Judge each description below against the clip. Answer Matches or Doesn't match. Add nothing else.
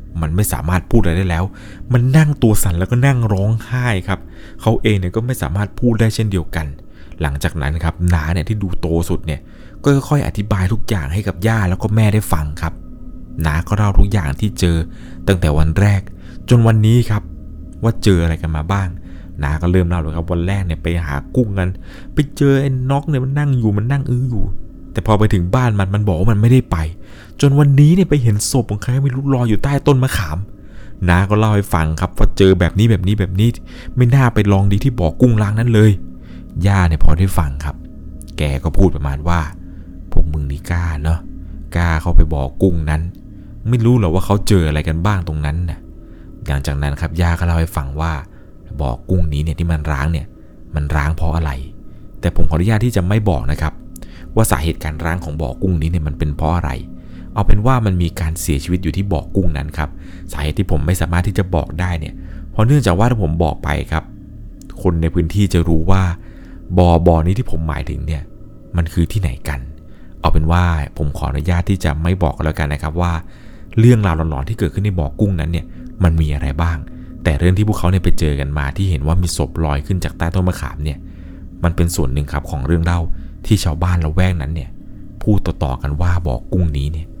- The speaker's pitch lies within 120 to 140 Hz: Doesn't match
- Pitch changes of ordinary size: Matches